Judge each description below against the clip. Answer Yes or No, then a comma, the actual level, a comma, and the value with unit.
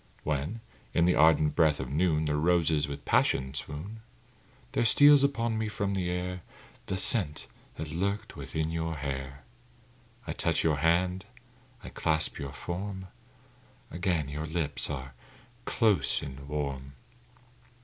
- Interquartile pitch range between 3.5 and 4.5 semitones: Yes, average, 4.2 semitones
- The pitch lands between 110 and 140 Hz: No, very low, 80 Hz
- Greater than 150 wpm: No, average, 140 wpm